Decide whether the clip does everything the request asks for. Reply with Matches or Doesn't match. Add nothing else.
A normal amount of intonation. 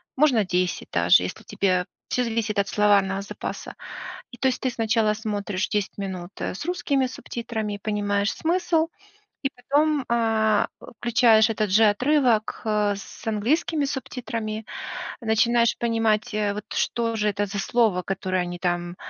Matches